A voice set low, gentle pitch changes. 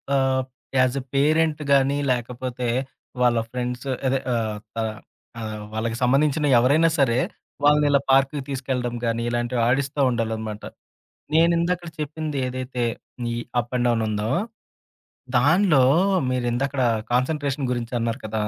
No: low, 130 Hz; average, 3.0 semitones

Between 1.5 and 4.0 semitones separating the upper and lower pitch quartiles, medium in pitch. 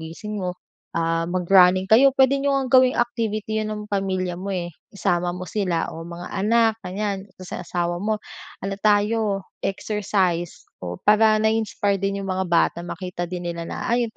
No: average, 3.4 semitones; high, 195 Hz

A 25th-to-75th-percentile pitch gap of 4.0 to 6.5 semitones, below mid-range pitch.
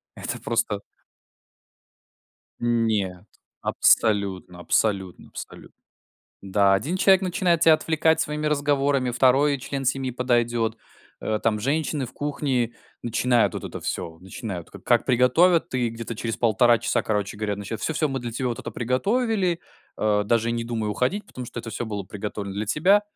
Yes: average, 5.1 semitones; low, 120 Hz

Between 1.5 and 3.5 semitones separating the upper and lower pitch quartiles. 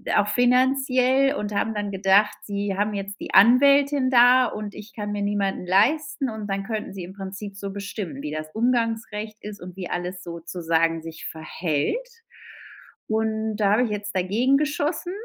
No: average, 4.0 semitones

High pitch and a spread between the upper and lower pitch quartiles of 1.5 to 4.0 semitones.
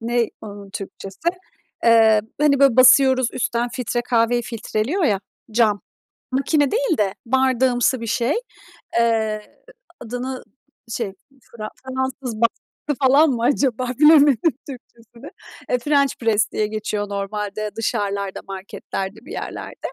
Yes: high, 235 Hz; average, 3.5 semitones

